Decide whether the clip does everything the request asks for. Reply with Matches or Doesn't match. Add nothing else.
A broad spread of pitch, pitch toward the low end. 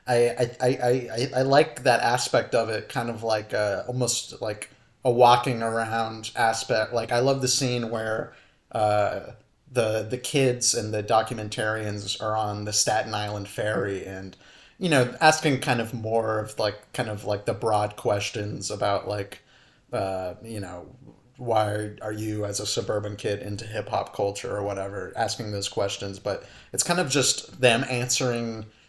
Doesn't match